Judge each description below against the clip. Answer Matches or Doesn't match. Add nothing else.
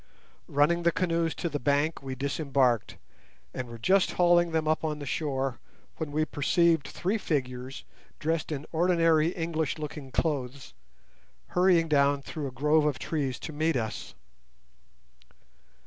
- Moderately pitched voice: Matches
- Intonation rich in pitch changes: Doesn't match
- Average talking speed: Matches